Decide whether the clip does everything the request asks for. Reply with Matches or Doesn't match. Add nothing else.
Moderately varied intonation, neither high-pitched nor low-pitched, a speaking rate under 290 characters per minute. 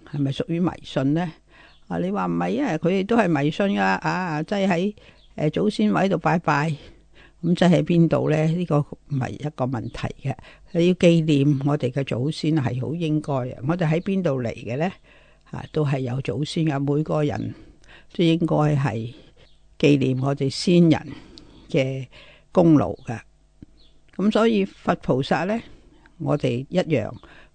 Matches